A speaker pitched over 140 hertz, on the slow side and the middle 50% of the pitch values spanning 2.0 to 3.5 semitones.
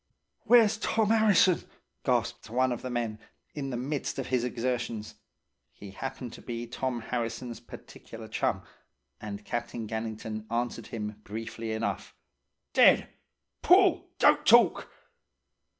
No: low, 120 Hz; slow, 125 wpm; narrow, 2.6 semitones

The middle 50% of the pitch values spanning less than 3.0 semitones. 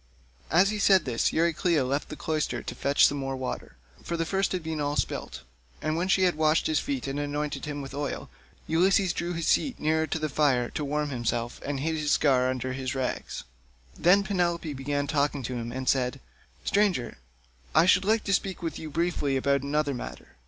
No: average, 4.0 semitones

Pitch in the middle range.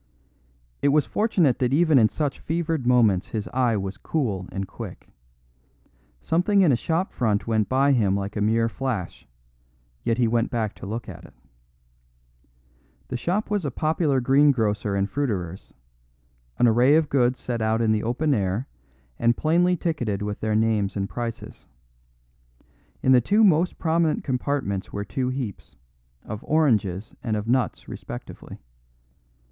No: low, 120 Hz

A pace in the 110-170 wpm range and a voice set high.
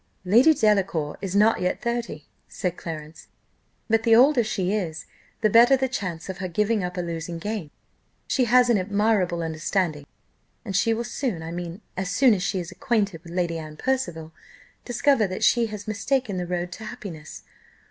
No: average, 180 wpm; high, 195 Hz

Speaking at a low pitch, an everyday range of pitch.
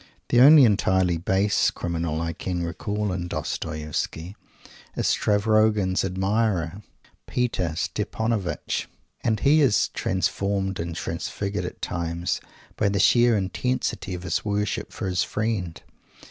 Yes: very low, 95 Hz; average, 3.6 semitones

